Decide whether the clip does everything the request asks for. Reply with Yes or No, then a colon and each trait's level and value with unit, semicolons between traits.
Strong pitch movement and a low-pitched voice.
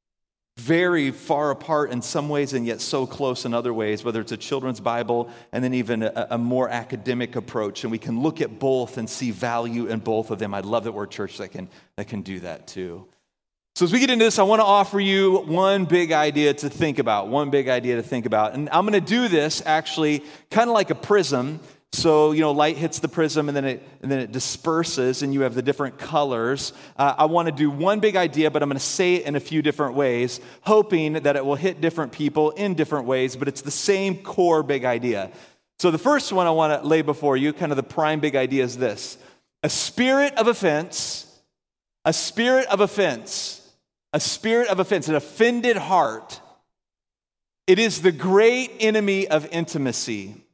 No: wide, 5.8 semitones; medium, 150 Hz